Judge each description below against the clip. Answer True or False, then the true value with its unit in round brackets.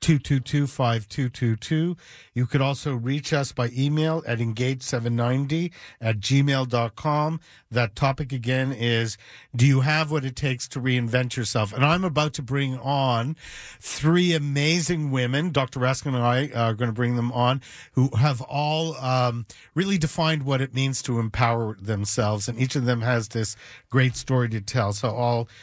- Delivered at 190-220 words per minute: False (175 wpm)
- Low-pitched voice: True (130 Hz)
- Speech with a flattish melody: False (3.2 semitones)